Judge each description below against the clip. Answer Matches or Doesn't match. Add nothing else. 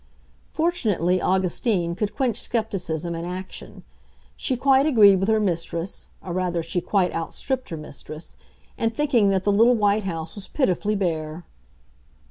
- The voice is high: Matches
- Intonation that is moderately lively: Matches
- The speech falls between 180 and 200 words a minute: Doesn't match